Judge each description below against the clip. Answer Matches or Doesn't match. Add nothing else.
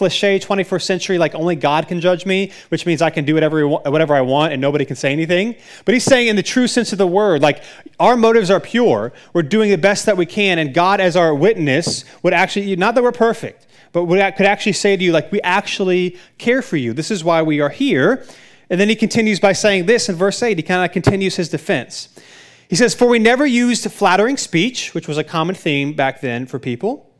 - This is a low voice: Doesn't match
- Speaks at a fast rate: Matches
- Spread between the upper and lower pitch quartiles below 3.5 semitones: Doesn't match